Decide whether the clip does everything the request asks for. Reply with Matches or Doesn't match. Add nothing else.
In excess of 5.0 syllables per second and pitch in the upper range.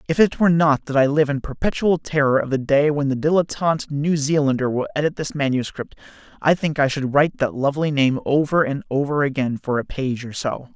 Doesn't match